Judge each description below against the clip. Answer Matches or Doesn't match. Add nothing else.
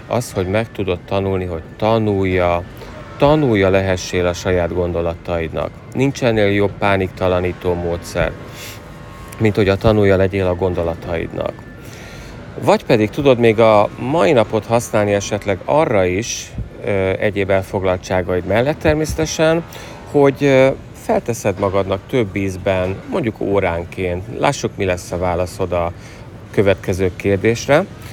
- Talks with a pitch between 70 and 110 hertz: Matches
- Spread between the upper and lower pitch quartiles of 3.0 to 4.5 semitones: Matches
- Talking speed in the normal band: Matches